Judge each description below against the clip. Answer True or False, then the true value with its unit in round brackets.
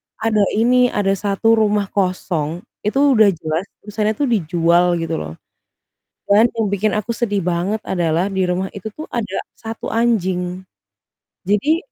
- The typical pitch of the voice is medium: False (200 Hz)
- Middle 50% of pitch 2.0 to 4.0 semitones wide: True (3.7 semitones)